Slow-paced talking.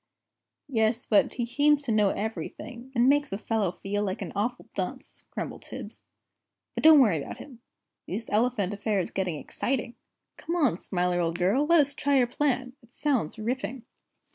No: average, 170 wpm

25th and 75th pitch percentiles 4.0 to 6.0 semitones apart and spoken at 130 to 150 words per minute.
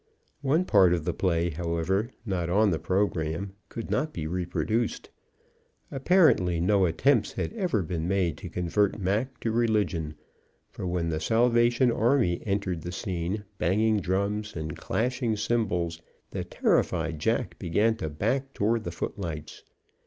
Yes: average, 5.0 semitones; average, 145 wpm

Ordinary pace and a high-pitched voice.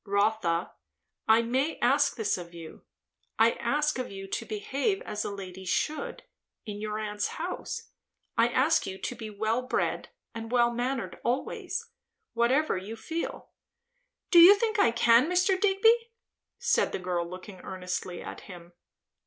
Yes: average, 155 wpm; high, 230 Hz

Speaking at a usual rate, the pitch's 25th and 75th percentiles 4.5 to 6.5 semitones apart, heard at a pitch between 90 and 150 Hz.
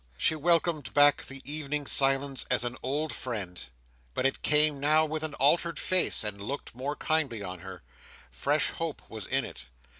No: average, 175 wpm; average, 4.0 semitones; medium, 140 Hz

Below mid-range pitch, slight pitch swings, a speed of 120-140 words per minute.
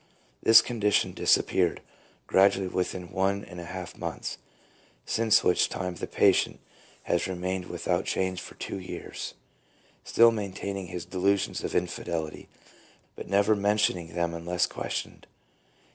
Yes: very low, 95 Hz; narrow, 2.0 semitones; slow, 135 wpm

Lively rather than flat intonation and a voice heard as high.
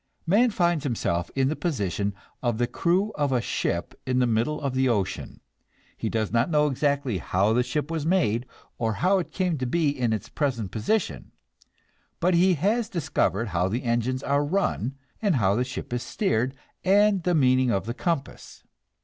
No: wide, 6.5 semitones; low, 130 Hz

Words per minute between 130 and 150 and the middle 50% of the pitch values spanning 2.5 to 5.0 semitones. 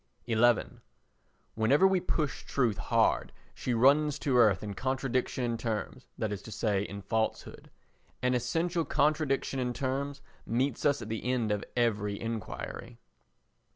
Yes: average, 145 wpm; average, 4.0 semitones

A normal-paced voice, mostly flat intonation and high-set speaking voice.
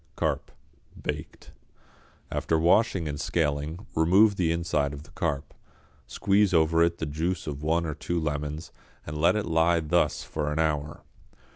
No: average, 155 wpm; narrow, 2.3 semitones; very low, 80 Hz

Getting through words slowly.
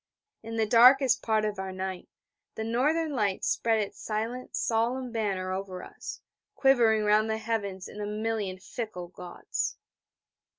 No: average, 145 wpm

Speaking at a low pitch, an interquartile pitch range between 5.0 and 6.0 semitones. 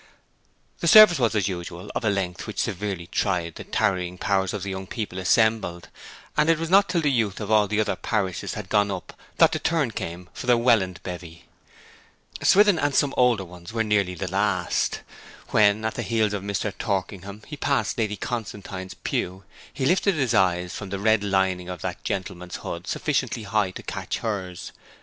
No: low, 100 Hz; average, 3.7 semitones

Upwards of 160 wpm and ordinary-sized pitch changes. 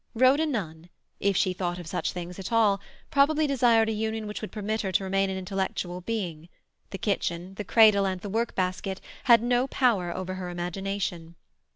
Yes: average, 190 wpm; average, 3.5 semitones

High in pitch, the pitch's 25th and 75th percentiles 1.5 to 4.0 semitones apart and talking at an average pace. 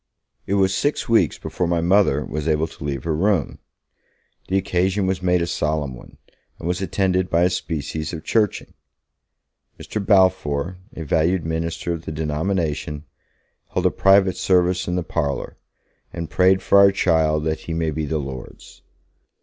No: very low, 85 Hz; average, 3.3 semitones; average, 165 wpm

